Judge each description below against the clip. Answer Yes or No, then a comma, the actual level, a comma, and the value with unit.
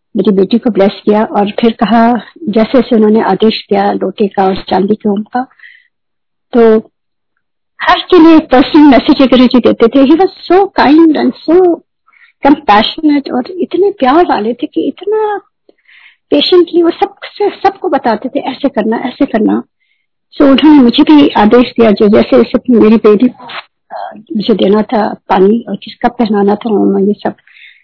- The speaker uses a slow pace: No, average, 150 wpm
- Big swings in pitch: Yes, wide, 6.9 semitones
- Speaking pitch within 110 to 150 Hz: No, very high, 250 Hz